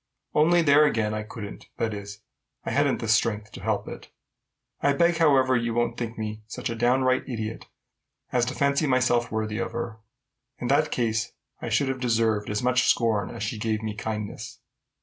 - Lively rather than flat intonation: No, average, 3.0 semitones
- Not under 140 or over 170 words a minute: No, average, 190 wpm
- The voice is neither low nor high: No, low, 115 Hz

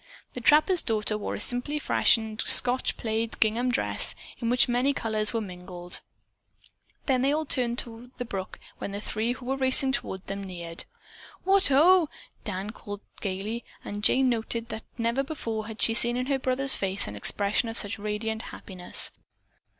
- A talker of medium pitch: No, high, 230 Hz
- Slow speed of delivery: No, average, 170 wpm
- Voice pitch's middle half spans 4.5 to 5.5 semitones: No, average, 3.6 semitones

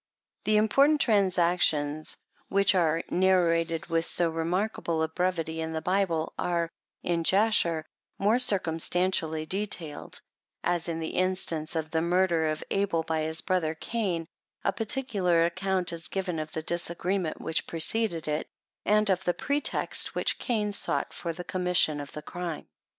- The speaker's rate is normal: Yes, average, 150 wpm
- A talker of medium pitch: Yes, medium, 175 Hz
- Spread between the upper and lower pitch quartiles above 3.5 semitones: No, average, 2.9 semitones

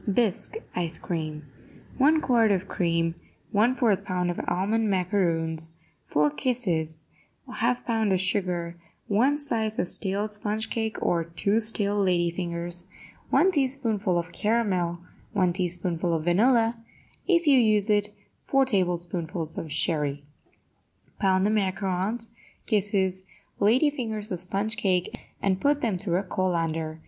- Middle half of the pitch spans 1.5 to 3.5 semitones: No, average, 4.4 semitones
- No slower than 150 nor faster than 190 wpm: No, slow, 135 wpm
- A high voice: Yes, high, 195 Hz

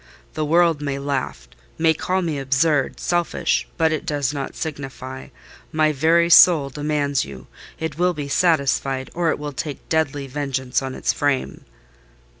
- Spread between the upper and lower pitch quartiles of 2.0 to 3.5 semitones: Yes, average, 2.9 semitones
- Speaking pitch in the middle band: Yes, medium, 145 Hz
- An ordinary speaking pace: Yes, average, 145 wpm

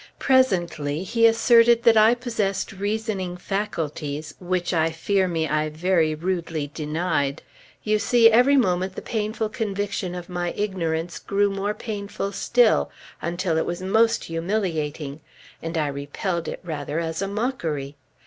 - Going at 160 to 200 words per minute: No, average, 140 wpm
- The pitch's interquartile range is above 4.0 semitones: Yes, average, 4.7 semitones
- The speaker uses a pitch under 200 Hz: Yes, medium, 185 Hz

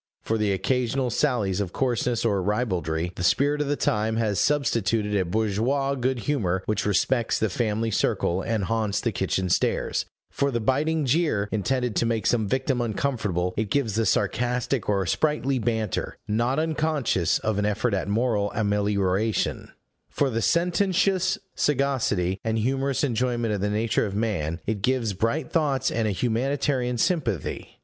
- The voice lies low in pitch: Yes, low, 115 Hz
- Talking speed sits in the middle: Yes, average, 160 wpm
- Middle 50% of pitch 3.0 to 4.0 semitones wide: No, average, 4.4 semitones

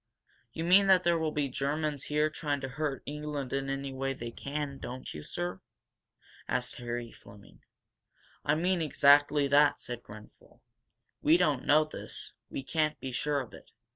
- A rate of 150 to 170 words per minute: Yes, average, 165 wpm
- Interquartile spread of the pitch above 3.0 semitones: No, narrow, 2.5 semitones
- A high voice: No, medium, 145 Hz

